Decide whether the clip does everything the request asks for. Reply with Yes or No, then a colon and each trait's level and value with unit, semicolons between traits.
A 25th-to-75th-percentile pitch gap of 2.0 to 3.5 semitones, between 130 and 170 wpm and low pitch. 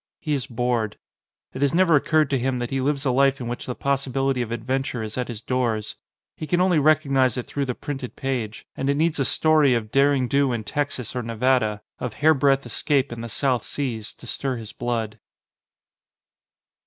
No: average, 2.9 semitones; average, 200 wpm; low, 130 Hz